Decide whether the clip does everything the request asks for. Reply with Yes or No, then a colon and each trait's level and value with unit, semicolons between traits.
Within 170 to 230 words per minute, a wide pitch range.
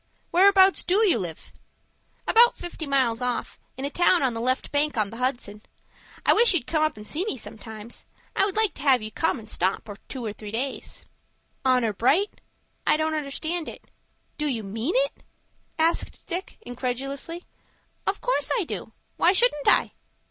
Yes: average, 175 wpm; wide, 7.1 semitones